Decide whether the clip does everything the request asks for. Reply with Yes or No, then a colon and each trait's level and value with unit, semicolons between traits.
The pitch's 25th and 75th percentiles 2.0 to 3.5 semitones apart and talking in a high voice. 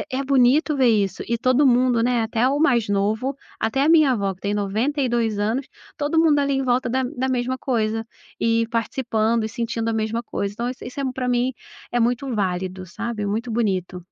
Yes: average, 3.1 semitones; high, 235 Hz